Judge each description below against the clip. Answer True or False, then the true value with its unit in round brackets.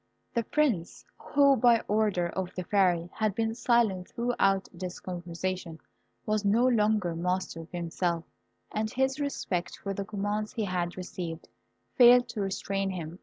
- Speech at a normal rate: True (150 wpm)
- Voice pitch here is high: True (195 Hz)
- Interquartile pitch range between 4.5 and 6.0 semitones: False (3.9 semitones)